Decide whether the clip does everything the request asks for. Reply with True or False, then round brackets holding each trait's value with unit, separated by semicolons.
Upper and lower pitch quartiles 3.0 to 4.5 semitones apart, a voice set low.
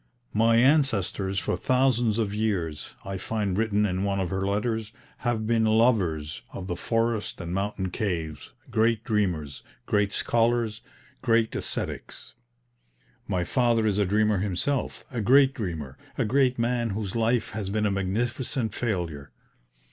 True (3.3 semitones; 105 Hz)